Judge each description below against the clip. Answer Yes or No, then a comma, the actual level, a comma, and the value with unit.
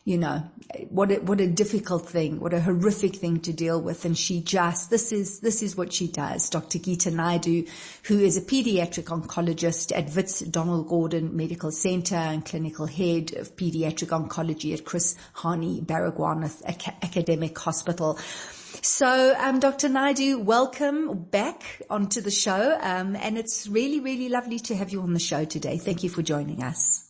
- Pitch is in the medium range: Yes, medium, 175 Hz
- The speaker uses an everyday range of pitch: Yes, average, 3.9 semitones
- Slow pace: No, average, 175 wpm